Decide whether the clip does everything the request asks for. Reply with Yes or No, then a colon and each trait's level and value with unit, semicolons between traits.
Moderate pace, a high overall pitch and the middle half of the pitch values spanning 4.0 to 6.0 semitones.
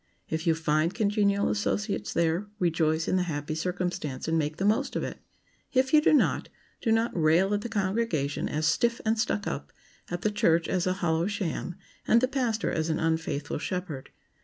No: average, 190 wpm; medium, 180 Hz; average, 4.7 semitones